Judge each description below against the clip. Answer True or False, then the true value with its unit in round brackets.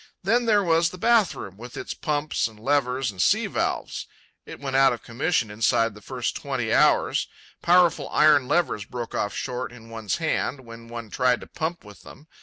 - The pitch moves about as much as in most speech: False (6.0 semitones)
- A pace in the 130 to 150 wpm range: False (190 wpm)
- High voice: False (130 Hz)